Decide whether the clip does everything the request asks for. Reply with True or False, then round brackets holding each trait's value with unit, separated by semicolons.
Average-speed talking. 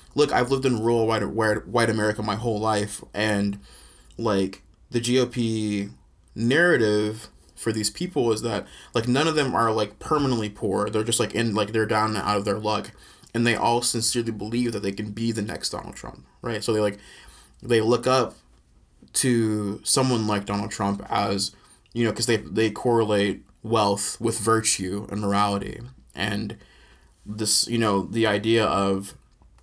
True (170 wpm)